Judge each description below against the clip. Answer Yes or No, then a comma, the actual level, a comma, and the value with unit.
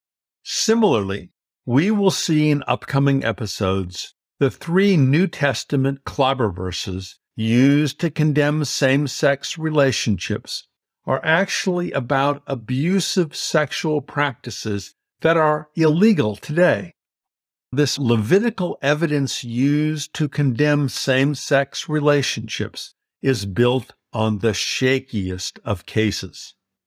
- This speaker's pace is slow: Yes, slow, 95 wpm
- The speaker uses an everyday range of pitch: Yes, average, 4.1 semitones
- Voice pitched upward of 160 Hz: No, medium, 140 Hz